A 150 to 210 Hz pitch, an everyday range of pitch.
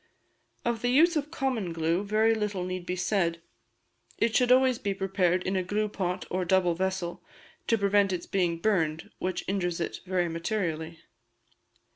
Yes: high, 190 Hz; average, 3.4 semitones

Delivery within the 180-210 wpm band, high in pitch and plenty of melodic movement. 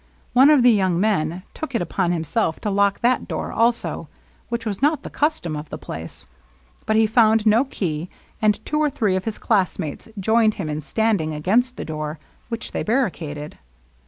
Yes: average, 190 wpm; high, 210 Hz; wide, 5.9 semitones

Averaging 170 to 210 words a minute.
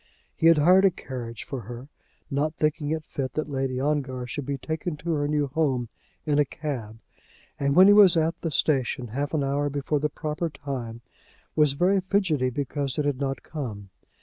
Yes: average, 195 wpm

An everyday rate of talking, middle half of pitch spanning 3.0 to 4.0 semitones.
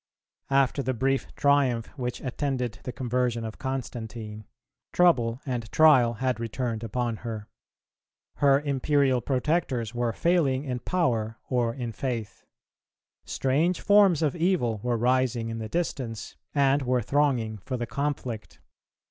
No: slow, 130 wpm; average, 3.3 semitones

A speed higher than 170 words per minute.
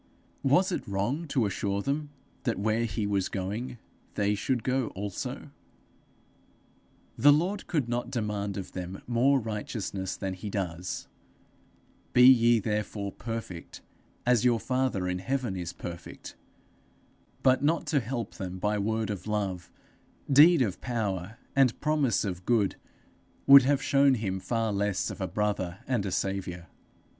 No: average, 145 wpm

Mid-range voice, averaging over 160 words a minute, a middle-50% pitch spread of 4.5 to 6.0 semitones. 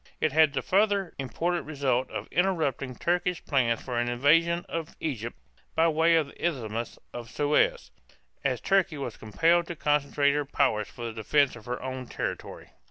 Yes: medium, 145 Hz; average, 170 wpm; average, 5.2 semitones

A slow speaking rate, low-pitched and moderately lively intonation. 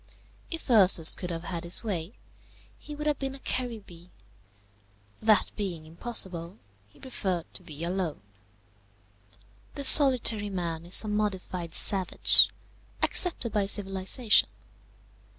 No: slow, 120 wpm; high, 195 Hz; average, 5.0 semitones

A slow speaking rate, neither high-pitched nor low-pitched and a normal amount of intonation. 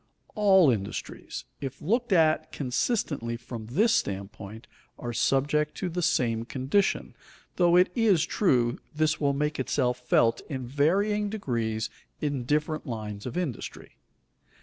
No: slow, 130 wpm; medium, 145 Hz; wide, 6.9 semitones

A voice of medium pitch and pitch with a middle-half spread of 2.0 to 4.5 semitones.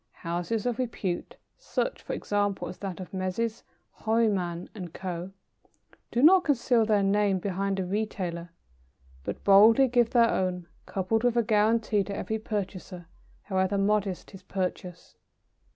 No: high, 200 Hz; average, 3.3 semitones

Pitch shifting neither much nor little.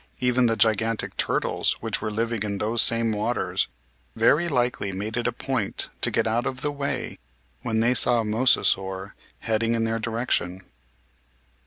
No: narrow, 2.1 semitones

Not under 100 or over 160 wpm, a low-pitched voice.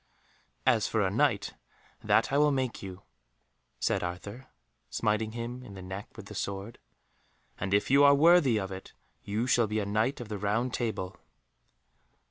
No: average, 170 wpm; low, 110 Hz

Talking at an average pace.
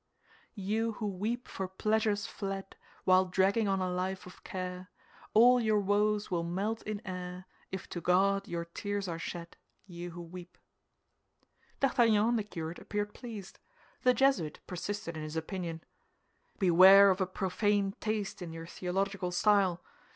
Yes: average, 150 wpm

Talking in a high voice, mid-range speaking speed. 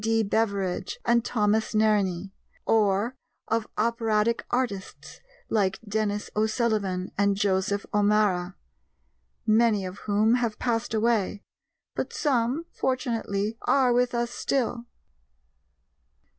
No: high, 215 Hz; slow, 105 wpm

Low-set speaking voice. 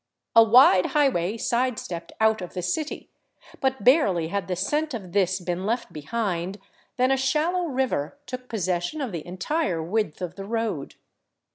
No: high, 210 Hz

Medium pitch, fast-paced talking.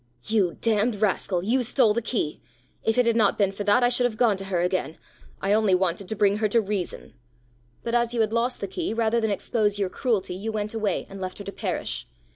No: high, 210 Hz; fast, 240 wpm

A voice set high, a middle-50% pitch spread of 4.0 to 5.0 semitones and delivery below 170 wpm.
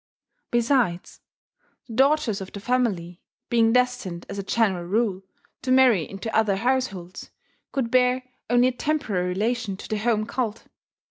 Yes: high, 225 Hz; average, 4.3 semitones; average, 145 wpm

